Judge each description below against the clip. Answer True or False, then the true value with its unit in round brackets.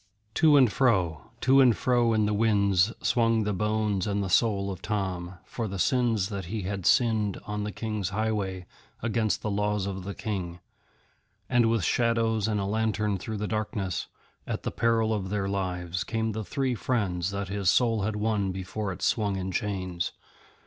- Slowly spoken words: False (185 wpm)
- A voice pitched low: True (105 Hz)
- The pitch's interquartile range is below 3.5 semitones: True (2.6 semitones)